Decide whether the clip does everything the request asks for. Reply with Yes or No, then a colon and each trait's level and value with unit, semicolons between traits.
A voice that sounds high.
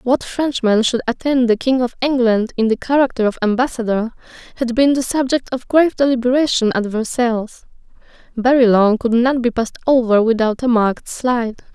Yes: high, 245 Hz